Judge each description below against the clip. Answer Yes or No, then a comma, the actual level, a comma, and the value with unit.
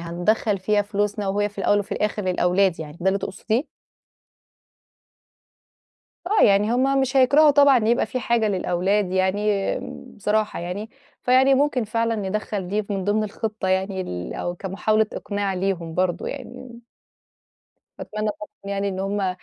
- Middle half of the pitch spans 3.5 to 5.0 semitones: No, average, 2.7 semitones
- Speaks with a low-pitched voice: No, high, 205 Hz